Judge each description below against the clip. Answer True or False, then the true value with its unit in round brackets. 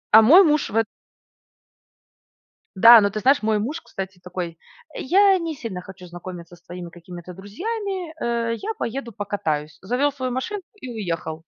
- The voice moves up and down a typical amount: False (8.0 semitones)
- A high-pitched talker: True (220 Hz)